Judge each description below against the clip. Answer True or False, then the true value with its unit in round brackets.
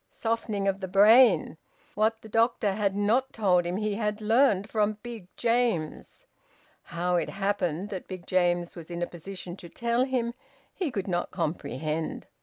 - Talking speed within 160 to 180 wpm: True (165 wpm)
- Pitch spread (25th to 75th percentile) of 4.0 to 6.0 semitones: True (4.3 semitones)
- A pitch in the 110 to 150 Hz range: False (200 Hz)